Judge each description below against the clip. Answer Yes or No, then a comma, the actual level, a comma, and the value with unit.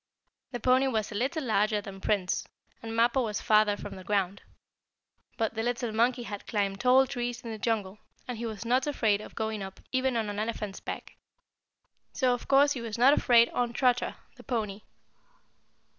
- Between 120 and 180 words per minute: No, average, 190 wpm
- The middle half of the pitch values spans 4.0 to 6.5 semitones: No, average, 2.9 semitones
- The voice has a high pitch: Yes, high, 230 Hz